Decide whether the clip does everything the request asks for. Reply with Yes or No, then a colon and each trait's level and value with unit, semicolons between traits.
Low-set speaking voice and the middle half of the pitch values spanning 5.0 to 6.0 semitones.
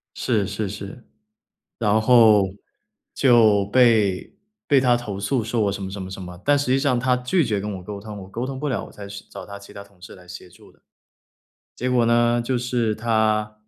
No: low, 110 Hz; average, 3.5 semitones